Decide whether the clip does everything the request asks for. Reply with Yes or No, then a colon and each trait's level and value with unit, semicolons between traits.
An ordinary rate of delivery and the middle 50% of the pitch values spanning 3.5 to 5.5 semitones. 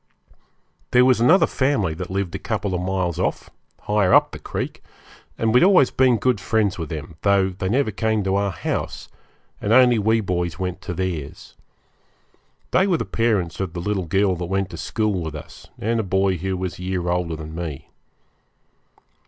Yes: average, 195 wpm; average, 3.9 semitones